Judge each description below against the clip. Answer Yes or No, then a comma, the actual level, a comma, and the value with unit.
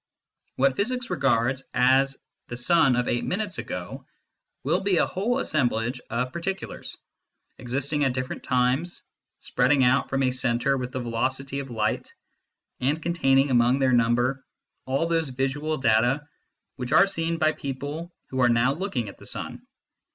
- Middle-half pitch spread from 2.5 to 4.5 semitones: Yes, average, 3.8 semitones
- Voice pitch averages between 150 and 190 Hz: No, low, 135 Hz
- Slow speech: No, average, 155 wpm